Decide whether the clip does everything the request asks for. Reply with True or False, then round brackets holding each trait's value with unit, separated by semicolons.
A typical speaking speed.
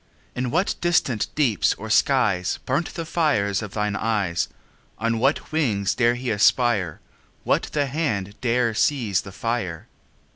True (150 wpm)